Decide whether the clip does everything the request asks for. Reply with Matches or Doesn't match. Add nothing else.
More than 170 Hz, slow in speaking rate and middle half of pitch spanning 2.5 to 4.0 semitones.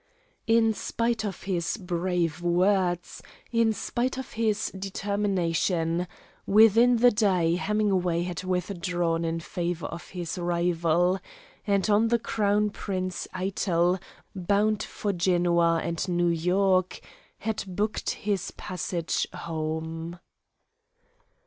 Matches